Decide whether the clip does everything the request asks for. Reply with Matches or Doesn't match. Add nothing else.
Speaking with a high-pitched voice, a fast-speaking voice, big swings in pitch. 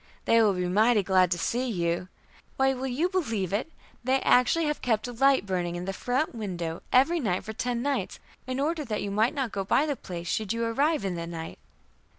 Matches